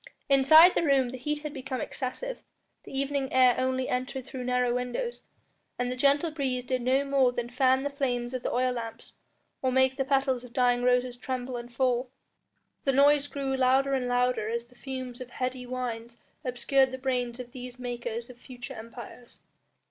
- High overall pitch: Yes, very high, 255 Hz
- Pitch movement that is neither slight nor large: No, narrow, 1.5 semitones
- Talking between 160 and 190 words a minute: Yes, average, 185 wpm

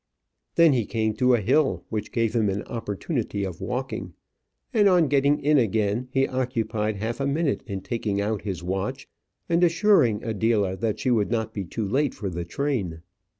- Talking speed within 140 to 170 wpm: No, average, 185 wpm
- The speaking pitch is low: Yes, low, 115 Hz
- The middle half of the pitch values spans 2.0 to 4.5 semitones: No, average, 4.9 semitones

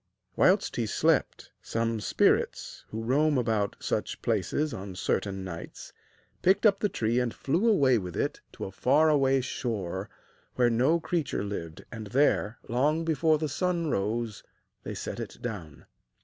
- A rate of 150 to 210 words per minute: Yes, average, 155 wpm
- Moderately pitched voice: No, low, 120 Hz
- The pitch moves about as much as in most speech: No, wide, 6.8 semitones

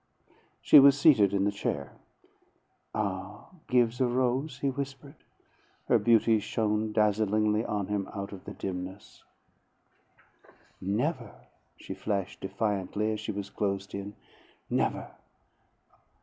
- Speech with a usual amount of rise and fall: Yes, average, 3.4 semitones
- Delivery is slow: Yes, slow, 120 wpm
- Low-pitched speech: Yes, low, 105 Hz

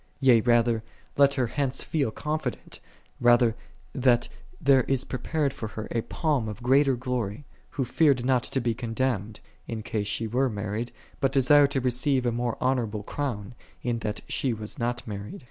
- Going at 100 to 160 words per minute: No, average, 170 wpm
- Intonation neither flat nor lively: Yes, average, 3.1 semitones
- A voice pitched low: Yes, low, 125 Hz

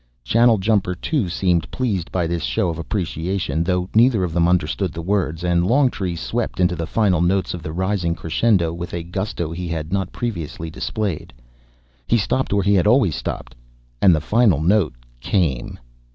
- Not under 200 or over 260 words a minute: No, average, 175 wpm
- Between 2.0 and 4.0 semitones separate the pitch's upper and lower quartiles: Yes, average, 3.5 semitones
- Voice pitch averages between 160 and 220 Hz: No, very low, 90 Hz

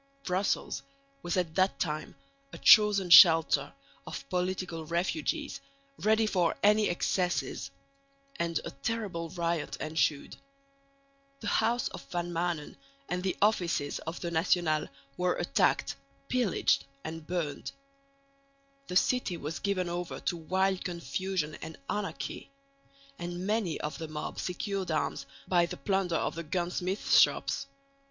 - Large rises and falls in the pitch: No, average, 2.7 semitones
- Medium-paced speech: No, slow, 130 wpm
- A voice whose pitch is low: No, medium, 175 Hz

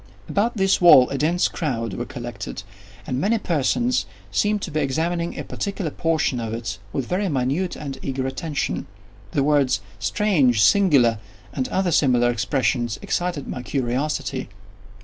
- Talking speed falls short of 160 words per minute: Yes, average, 150 wpm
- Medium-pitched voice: Yes, medium, 145 Hz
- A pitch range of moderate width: No, wide, 5.7 semitones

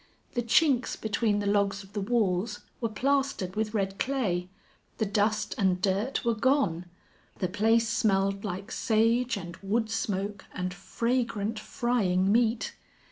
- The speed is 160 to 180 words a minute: No, average, 140 wpm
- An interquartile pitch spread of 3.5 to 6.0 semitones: No, average, 3.1 semitones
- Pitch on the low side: No, high, 210 Hz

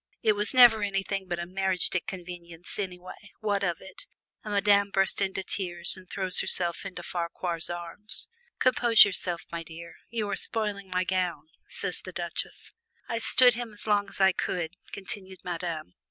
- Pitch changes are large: No, average, 2.8 semitones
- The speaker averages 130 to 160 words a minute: No, average, 175 wpm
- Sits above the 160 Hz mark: Yes, high, 190 Hz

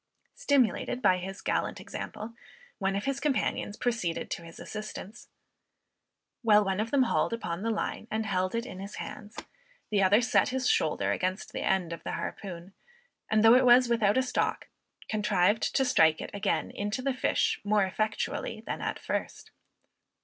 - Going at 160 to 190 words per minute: Yes, average, 170 wpm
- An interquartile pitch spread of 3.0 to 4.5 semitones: Yes, average, 3.8 semitones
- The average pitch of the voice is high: Yes, high, 210 Hz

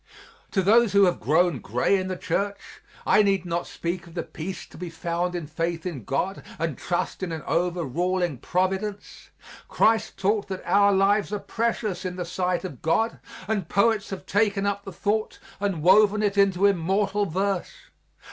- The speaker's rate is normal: Yes, average, 175 wpm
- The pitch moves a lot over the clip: No, average, 2.7 semitones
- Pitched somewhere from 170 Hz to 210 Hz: Yes, high, 190 Hz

